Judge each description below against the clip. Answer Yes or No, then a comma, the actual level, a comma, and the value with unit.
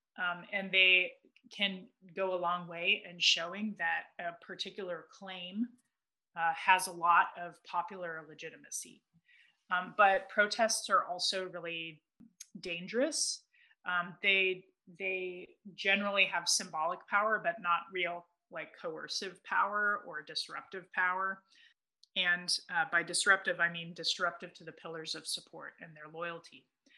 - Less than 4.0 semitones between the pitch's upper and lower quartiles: Yes, average, 2.8 semitones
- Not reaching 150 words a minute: Yes, average, 130 wpm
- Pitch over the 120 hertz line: Yes, medium, 185 Hz